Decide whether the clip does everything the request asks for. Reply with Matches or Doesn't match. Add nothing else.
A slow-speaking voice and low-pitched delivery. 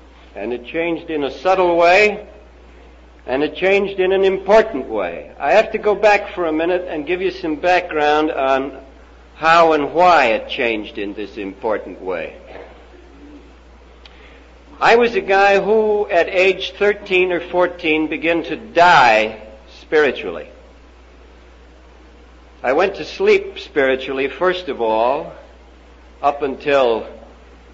Doesn't match